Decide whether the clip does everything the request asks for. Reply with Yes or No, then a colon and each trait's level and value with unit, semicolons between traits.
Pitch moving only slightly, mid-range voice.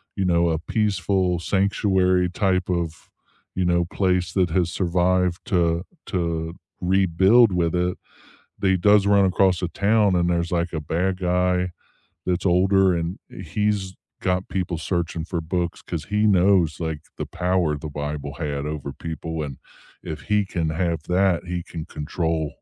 No: narrow, 2.2 semitones; very low, 90 Hz